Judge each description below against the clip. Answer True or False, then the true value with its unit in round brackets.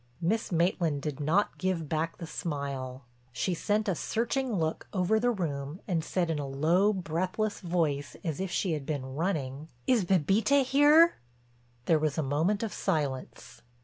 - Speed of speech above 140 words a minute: True (165 wpm)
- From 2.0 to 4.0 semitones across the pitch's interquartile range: False (5.3 semitones)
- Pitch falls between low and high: True (170 Hz)